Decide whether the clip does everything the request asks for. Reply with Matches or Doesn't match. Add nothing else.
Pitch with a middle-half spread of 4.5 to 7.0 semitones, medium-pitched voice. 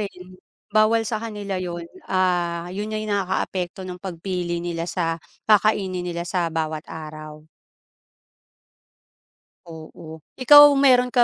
Doesn't match